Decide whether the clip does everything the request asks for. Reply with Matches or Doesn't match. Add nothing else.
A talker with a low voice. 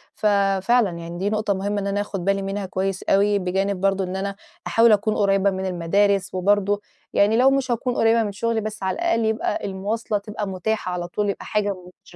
Doesn't match